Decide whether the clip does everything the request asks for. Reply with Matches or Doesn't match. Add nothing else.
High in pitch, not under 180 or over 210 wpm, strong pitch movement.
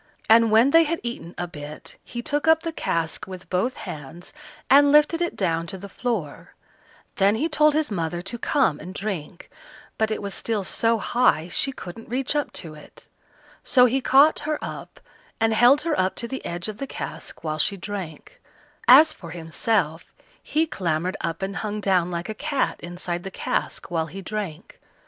Matches